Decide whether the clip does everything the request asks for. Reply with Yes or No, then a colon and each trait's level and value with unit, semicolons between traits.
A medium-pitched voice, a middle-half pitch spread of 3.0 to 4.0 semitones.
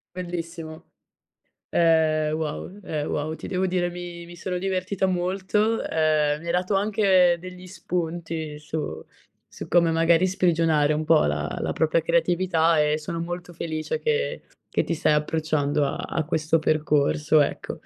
No: medium, 165 Hz; narrow, 2.6 semitones